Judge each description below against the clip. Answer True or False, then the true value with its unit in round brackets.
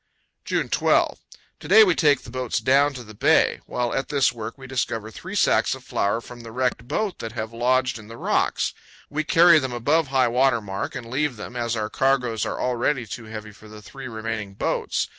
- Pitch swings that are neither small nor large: True (3.1 semitones)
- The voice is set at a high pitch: False (120 Hz)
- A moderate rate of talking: False (215 wpm)